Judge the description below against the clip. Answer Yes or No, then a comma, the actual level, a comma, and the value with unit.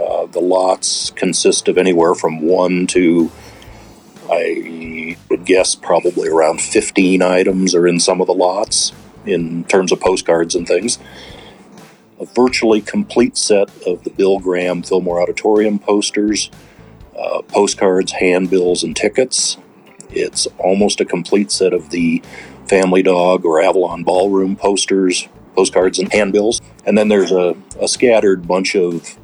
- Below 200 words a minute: Yes, average, 140 wpm